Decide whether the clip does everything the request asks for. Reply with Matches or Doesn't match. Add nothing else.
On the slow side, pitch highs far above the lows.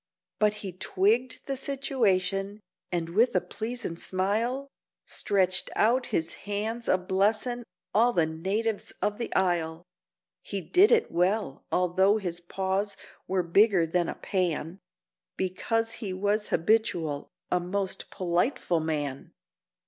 Doesn't match